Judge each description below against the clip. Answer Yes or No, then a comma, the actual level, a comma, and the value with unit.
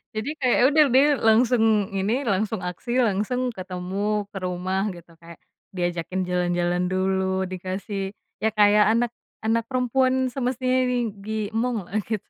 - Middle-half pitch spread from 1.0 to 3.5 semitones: No, average, 4.3 semitones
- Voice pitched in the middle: No, high, 205 Hz